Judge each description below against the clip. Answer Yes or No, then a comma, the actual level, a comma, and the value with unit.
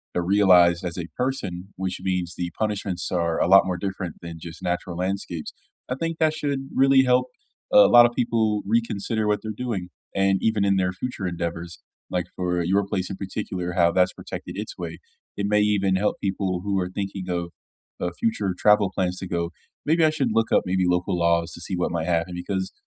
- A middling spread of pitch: Yes, average, 3.1 semitones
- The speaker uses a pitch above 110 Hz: No, very low, 95 Hz